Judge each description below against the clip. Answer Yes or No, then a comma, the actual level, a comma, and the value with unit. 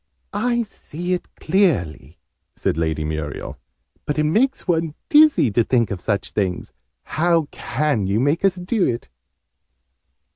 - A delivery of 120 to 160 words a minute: Yes, average, 140 wpm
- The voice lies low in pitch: No, medium, 150 Hz